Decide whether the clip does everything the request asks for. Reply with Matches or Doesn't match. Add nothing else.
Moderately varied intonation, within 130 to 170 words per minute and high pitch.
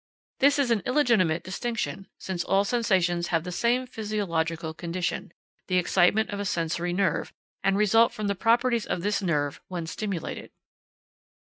Matches